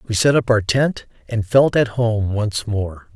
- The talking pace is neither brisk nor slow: No, fast, 210 wpm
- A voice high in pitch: No, low, 110 Hz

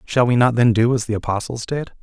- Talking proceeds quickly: Yes, fast, 265 wpm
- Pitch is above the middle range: No, low, 120 Hz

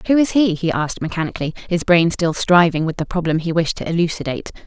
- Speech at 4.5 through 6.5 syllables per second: No, 6.7 syllables/s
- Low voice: No, medium, 170 Hz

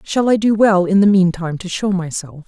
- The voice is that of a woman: Yes, female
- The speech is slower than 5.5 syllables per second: Yes, 5.1 syllables/s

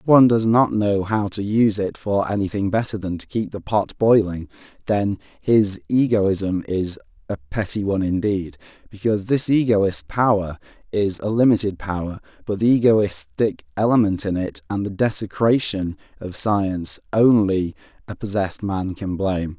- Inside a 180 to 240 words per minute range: No, average, 155 wpm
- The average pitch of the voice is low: Yes, low, 100 Hz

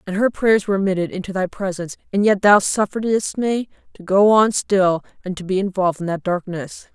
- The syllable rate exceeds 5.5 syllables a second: Yes, 5.7 syllables/s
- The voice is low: No, high, 190 Hz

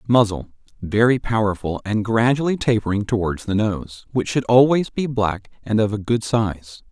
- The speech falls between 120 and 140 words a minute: No, average, 155 wpm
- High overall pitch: No, low, 110 Hz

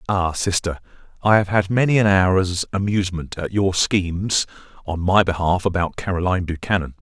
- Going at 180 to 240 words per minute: No, average, 155 wpm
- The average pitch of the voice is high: No, very low, 95 Hz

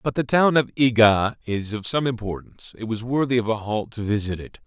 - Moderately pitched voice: No, low, 115 Hz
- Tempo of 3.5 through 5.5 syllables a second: No, 5.7 syllables/s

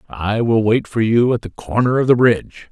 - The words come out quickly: Yes, fast, 245 wpm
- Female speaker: No, male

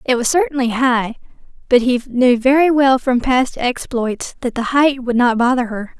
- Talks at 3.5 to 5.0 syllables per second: Yes, 4.6 syllables/s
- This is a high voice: Yes, very high, 250 Hz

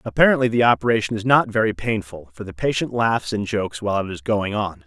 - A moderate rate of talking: No, fast, 220 wpm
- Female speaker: No, male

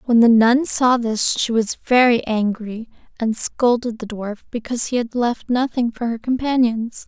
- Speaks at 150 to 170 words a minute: No, average, 180 wpm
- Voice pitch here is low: No, high, 235 Hz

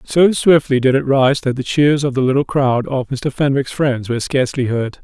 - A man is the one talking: Yes, male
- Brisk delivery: Yes, fast, 225 wpm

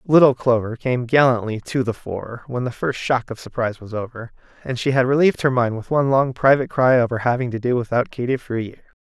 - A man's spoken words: Yes, male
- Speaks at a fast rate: Yes, fast, 230 wpm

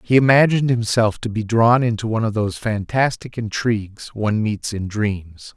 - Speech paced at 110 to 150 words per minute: No, average, 175 wpm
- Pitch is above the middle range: No, low, 110 Hz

